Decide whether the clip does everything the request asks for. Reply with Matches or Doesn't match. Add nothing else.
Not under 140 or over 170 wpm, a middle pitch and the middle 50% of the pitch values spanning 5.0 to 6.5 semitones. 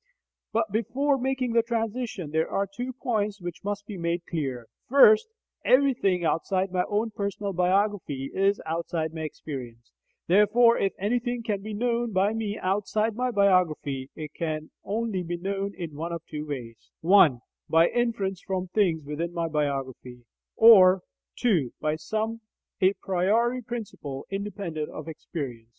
Doesn't match